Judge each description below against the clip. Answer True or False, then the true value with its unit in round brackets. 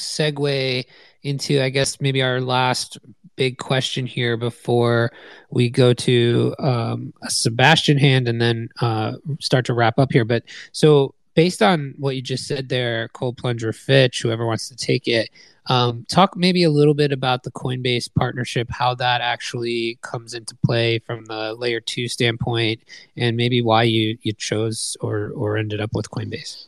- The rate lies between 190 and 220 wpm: False (170 wpm)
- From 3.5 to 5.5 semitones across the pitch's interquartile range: False (2.7 semitones)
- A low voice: True (125 Hz)